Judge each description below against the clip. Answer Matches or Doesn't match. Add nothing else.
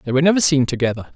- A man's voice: Matches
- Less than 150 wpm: Doesn't match